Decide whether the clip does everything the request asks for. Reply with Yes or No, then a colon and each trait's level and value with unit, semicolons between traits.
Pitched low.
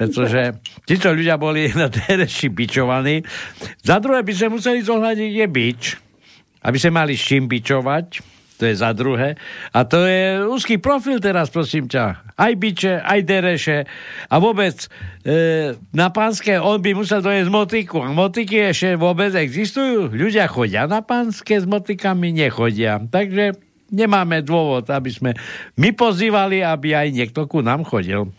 No: medium, 170 Hz